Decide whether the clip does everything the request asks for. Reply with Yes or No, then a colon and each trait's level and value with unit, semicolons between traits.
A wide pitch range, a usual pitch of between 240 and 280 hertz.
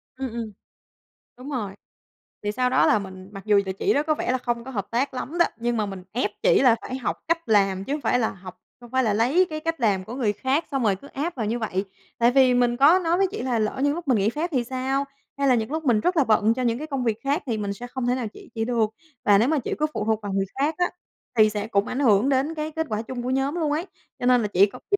No: average, 4.7 semitones; high, 245 Hz